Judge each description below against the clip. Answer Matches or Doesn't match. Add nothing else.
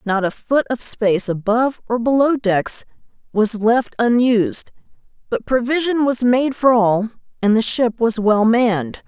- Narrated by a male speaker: Doesn't match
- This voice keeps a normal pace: Matches